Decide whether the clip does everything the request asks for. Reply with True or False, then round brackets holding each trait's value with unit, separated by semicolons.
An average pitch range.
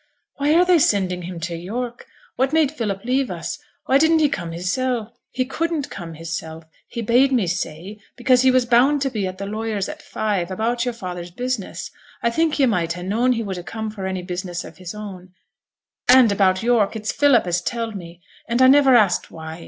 False (5.9 semitones)